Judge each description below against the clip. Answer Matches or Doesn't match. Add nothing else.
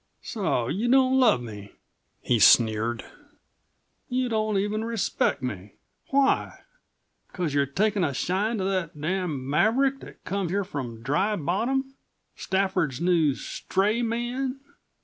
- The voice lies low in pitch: Doesn't match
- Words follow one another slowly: Matches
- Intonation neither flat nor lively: Doesn't match